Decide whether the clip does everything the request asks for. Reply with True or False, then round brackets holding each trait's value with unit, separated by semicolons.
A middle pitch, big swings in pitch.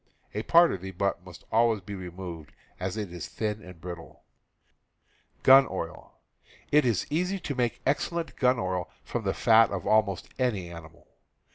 False (100 Hz; 5.7 semitones)